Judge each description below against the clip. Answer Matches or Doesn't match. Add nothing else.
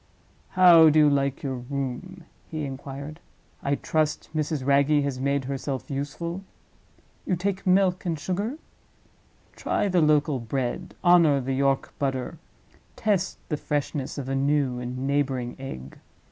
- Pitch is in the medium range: Matches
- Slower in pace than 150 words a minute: Matches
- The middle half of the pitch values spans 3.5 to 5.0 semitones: Matches